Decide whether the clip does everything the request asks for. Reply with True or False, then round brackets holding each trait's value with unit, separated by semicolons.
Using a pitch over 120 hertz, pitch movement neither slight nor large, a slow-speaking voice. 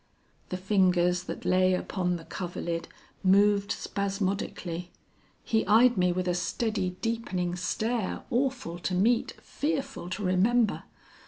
True (185 Hz; 3.5 semitones; 120 wpm)